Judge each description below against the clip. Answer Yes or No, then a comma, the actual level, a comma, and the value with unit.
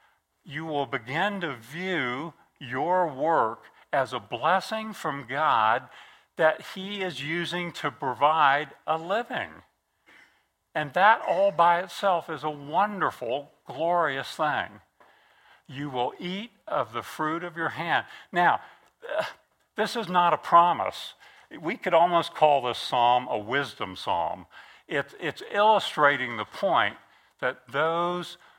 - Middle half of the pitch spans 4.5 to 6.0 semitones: No, average, 4.1 semitones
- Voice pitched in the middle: Yes, medium, 165 Hz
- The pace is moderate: No, slow, 125 wpm